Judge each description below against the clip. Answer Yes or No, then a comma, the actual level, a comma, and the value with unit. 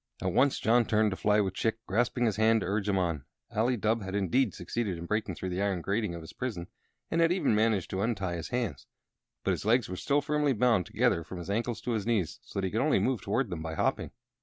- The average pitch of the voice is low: Yes, low, 105 Hz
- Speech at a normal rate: No, fast, 255 wpm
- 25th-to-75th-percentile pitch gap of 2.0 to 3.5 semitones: No, average, 4.2 semitones